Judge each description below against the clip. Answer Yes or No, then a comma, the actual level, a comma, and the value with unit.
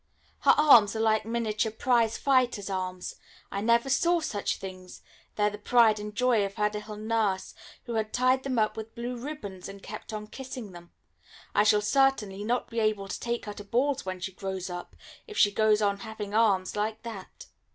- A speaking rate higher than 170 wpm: Yes, average, 200 wpm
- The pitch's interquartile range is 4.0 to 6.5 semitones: No, average, 2.8 semitones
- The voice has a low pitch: No, high, 215 Hz